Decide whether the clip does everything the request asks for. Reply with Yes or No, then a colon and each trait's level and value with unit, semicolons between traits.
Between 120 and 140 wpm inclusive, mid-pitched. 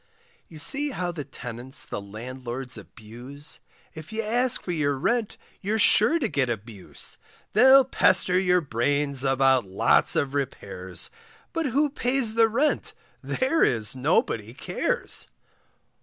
Yes: slow, 135 wpm; medium, 145 Hz